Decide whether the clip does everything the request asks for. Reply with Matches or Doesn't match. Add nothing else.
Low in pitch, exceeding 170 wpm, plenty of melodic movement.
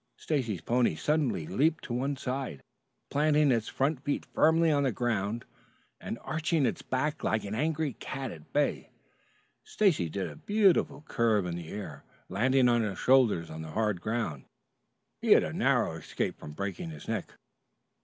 Doesn't match